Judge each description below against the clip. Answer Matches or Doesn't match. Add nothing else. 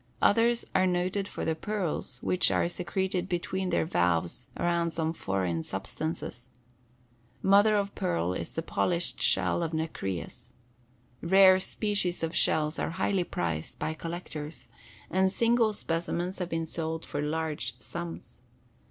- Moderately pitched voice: Matches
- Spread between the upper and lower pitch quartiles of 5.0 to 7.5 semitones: Doesn't match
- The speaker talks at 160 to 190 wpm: Doesn't match